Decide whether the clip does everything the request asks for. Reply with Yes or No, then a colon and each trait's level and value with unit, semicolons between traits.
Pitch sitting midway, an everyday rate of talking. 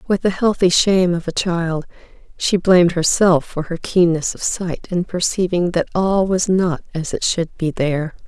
Yes: medium, 175 Hz; average, 190 wpm